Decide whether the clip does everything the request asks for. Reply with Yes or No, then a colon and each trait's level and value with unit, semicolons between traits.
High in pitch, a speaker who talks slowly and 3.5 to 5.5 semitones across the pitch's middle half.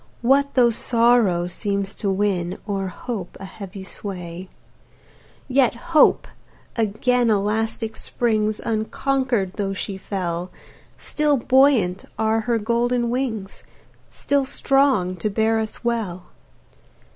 Yes: high, 220 Hz; slow, 110 wpm; average, 4.0 semitones